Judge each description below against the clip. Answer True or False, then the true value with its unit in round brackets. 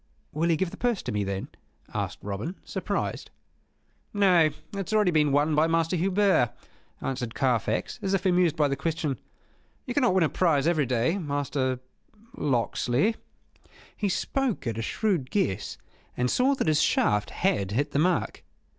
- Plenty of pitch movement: True (6.6 semitones)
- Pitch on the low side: False (155 Hz)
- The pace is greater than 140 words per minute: True (165 wpm)